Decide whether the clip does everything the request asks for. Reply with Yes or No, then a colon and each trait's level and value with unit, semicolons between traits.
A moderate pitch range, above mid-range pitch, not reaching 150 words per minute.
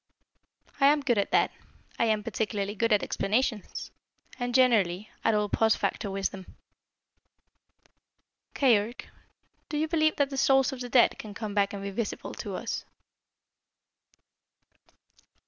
Yes: average, 4.3 semitones; high, 225 Hz; average, 140 wpm